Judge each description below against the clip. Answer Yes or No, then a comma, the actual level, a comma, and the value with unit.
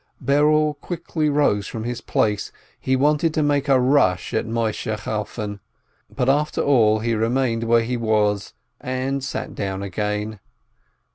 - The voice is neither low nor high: No, low, 120 Hz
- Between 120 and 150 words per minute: Yes, average, 145 wpm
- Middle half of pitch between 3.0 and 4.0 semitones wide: No, average, 4.9 semitones